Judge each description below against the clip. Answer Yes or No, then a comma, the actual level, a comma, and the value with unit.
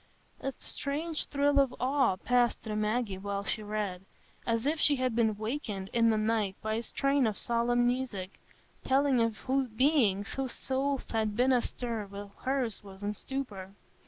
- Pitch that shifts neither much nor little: Yes, average, 4.2 semitones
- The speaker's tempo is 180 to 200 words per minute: No, average, 165 wpm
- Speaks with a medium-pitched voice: No, high, 230 Hz